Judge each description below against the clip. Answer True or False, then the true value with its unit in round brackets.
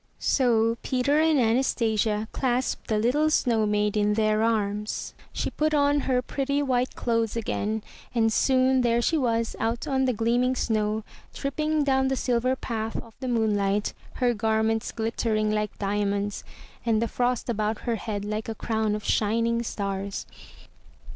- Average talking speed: True (155 wpm)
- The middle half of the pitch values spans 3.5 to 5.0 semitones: False (3.0 semitones)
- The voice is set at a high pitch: True (230 Hz)